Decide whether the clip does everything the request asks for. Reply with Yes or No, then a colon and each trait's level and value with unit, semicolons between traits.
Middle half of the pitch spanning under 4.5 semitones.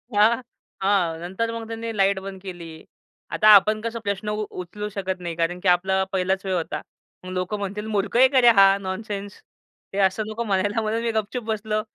Yes: narrow, 2.4 semitones